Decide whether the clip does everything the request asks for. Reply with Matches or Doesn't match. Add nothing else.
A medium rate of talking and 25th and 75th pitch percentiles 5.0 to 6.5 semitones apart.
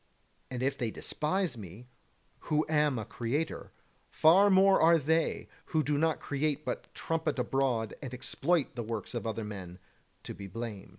Matches